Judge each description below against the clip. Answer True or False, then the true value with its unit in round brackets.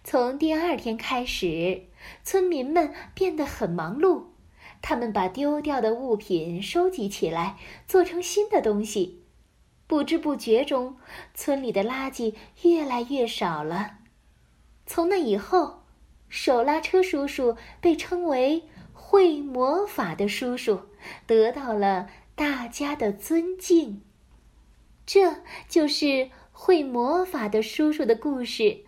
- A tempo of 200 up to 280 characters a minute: False (175 characters per minute)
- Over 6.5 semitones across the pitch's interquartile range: True (7.4 semitones)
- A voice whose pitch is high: True (270 Hz)